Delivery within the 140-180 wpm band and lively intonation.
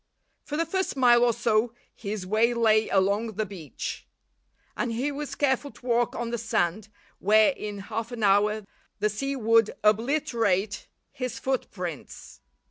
No: average, 150 wpm; average, 2.7 semitones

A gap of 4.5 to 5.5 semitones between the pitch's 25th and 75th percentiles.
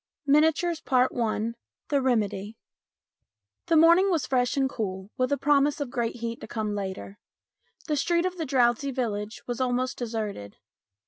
Yes: average, 4.8 semitones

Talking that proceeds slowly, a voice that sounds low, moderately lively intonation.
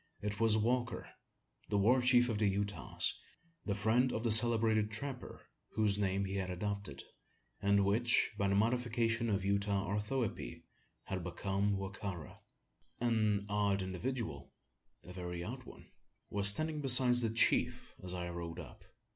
No: average, 155 wpm; low, 105 Hz; average, 3.1 semitones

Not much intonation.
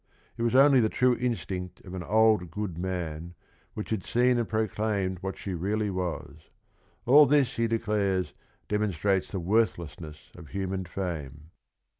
No: average, 3.8 semitones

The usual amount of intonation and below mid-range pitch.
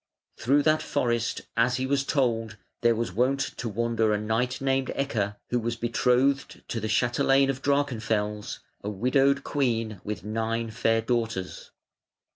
Yes: average, 3.2 semitones; low, 120 Hz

